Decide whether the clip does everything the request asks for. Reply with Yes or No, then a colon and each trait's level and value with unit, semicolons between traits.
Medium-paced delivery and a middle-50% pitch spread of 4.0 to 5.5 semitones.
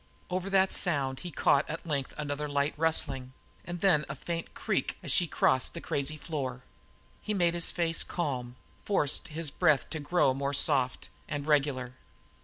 No: average, 170 wpm; average, 3.6 semitones